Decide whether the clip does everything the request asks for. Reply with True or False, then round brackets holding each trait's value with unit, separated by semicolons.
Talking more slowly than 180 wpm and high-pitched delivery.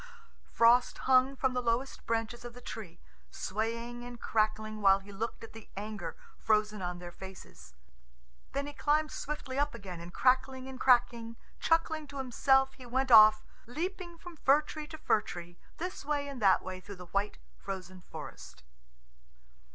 True (165 wpm; 235 Hz)